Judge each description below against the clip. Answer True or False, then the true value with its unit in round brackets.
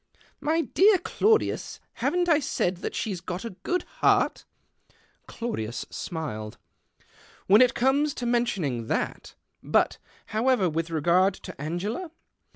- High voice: True (210 Hz)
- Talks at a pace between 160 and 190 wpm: False (145 wpm)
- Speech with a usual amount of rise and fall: False (8.7 semitones)